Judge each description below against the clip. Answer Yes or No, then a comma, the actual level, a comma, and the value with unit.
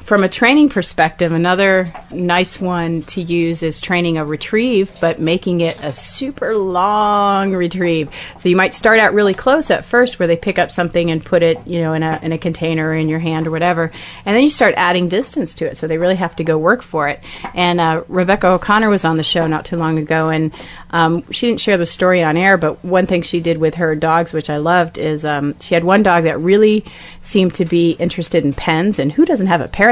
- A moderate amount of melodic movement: Yes, average, 3.1 semitones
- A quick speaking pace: Yes, fast, 235 wpm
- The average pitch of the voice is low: No, medium, 175 Hz